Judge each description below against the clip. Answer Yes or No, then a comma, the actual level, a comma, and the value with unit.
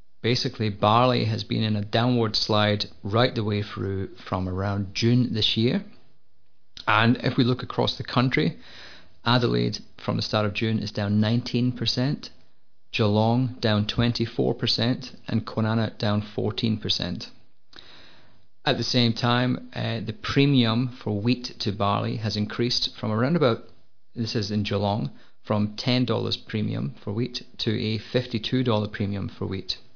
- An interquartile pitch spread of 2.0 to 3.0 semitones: Yes, narrow, 2.6 semitones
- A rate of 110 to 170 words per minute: Yes, average, 140 wpm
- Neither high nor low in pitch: No, low, 110 Hz